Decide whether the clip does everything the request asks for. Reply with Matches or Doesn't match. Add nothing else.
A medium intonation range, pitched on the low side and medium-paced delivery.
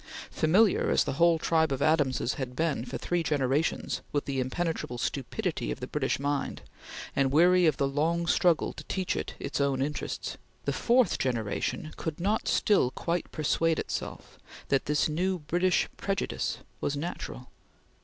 Doesn't match